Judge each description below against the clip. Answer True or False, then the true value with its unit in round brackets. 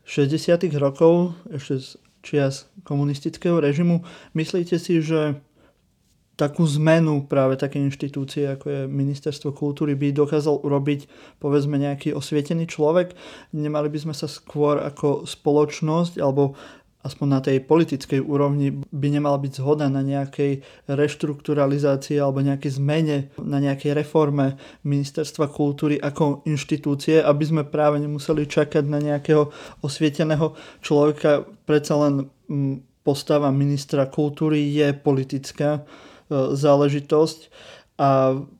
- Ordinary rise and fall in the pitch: False (1.5 semitones)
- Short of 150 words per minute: True (120 wpm)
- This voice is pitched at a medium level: True (145 Hz)